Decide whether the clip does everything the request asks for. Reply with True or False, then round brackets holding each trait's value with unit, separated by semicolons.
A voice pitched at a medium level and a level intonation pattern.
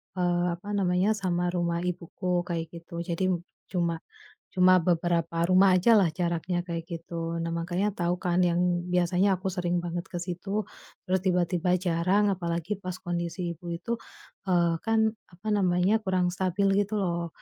True (180 Hz; 1.6 semitones)